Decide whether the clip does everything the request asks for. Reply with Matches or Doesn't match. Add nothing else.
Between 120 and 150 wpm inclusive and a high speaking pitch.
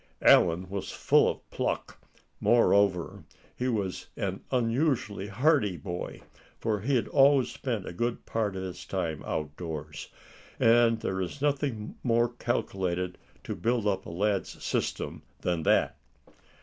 Doesn't match